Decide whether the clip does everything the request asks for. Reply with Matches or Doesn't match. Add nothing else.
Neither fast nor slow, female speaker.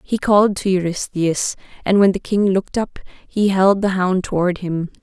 Matches